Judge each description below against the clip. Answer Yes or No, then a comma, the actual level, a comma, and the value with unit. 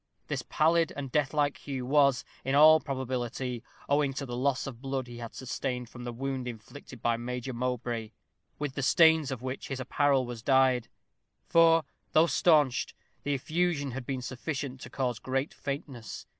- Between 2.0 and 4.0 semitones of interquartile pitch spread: Yes, narrow, 2.5 semitones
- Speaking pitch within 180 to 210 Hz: No, low, 135 Hz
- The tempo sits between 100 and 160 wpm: No, average, 170 wpm